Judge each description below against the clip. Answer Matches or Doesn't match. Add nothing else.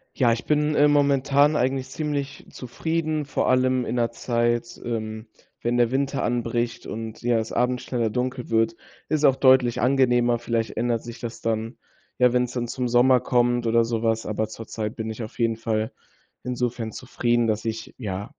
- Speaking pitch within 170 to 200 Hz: Doesn't match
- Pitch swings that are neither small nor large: Doesn't match